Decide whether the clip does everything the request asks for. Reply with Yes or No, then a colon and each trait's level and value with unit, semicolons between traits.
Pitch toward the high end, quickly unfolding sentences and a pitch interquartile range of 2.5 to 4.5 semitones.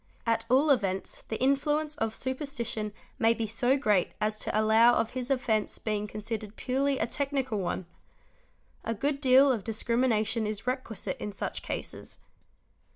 No: high, 230 Hz; average, 160 wpm; average, 3.6 semitones